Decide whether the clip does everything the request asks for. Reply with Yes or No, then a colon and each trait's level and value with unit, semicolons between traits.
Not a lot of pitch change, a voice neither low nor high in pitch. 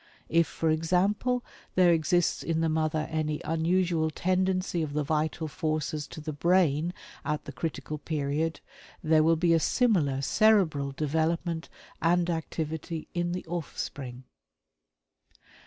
Yes: narrow, 2.2 semitones; medium, 160 Hz